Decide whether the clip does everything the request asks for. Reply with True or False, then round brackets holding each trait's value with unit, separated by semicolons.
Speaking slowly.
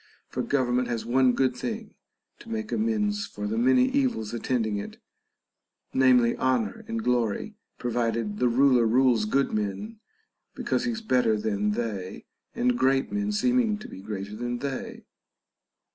False (155 wpm)